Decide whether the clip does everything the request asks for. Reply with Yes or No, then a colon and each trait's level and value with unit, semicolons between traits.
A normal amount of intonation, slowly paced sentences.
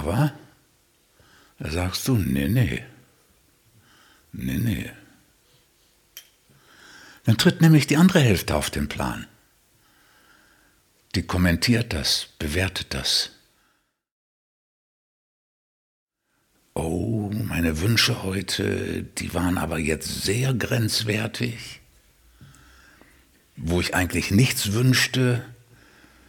No: wide, 5.9 semitones; slow, 85 wpm